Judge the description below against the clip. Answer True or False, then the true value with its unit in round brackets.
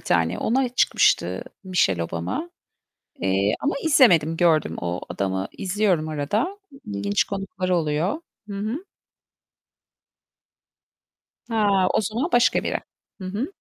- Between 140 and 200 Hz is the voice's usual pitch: True (185 Hz)